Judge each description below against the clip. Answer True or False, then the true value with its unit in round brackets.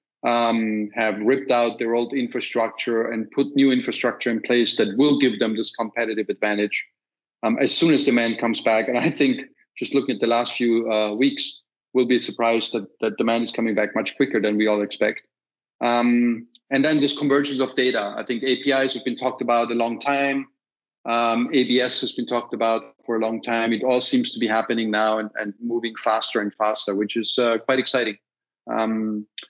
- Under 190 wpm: False (200 wpm)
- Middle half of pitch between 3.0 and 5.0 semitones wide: False (2.4 semitones)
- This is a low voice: True (115 Hz)